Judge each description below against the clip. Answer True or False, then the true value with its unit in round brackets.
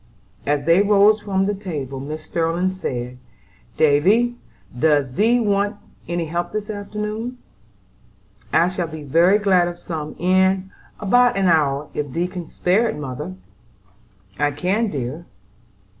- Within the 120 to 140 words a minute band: True (135 wpm)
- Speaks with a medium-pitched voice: True (175 Hz)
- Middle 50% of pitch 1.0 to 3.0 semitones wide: False (5.2 semitones)